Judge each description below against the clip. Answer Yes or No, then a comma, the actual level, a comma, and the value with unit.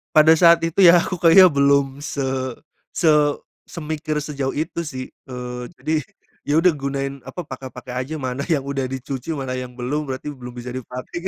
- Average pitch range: Yes, average, 3.4 semitones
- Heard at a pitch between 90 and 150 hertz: Yes, medium, 140 Hz